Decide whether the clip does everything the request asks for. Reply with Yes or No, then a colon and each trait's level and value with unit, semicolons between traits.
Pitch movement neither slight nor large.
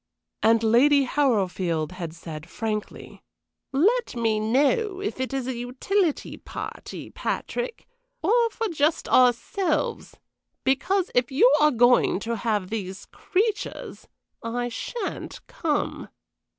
No: wide, 7.1 semitones